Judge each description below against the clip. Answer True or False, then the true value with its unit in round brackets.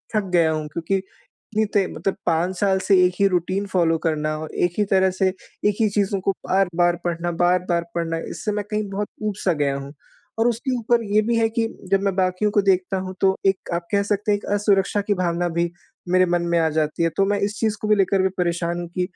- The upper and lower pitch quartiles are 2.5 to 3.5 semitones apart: True (3.0 semitones)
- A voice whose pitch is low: False (190 Hz)